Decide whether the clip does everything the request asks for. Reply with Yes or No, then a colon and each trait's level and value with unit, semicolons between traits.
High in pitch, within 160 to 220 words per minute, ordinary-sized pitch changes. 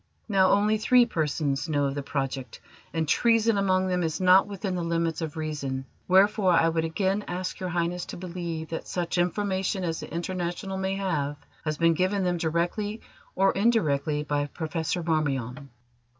No: medium, 175 Hz; average, 170 wpm; average, 3.4 semitones